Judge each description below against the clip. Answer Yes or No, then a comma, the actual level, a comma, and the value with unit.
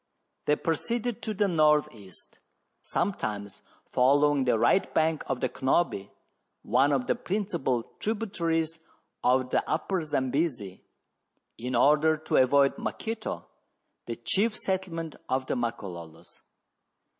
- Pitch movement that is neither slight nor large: No, wide, 6.1 semitones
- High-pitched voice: No, medium, 150 Hz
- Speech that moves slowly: Yes, slow, 120 wpm